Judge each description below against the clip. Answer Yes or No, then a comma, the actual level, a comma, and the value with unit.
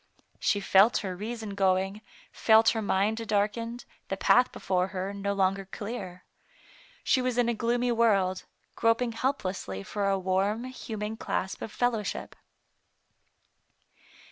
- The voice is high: Yes, high, 210 Hz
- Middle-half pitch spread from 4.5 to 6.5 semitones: No, average, 3.2 semitones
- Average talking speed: No, slow, 130 wpm